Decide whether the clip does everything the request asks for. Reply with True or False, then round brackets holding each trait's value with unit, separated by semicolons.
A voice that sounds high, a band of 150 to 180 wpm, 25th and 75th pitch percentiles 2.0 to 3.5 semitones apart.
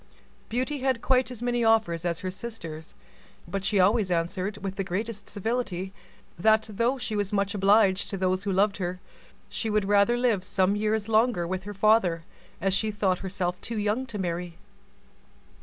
True (205 Hz; 170 wpm; 3.1 semitones)